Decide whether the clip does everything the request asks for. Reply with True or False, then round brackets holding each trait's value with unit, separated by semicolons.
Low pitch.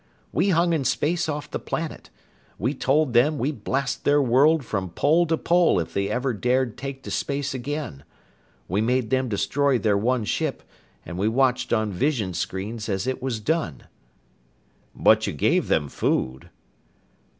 True (130 Hz)